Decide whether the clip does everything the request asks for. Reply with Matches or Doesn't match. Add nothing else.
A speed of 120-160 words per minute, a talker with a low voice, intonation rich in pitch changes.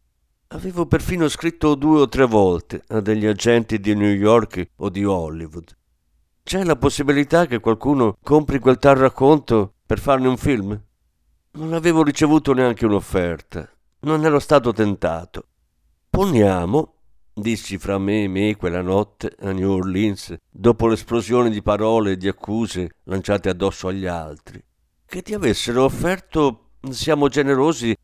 Matches